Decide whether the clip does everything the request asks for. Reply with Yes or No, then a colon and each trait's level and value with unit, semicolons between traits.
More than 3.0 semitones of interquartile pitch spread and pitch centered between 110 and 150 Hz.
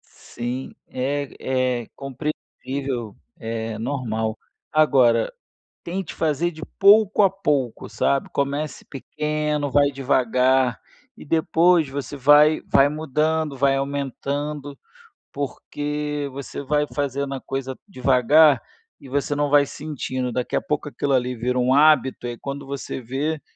No: narrow, 2.6 semitones; medium, 140 Hz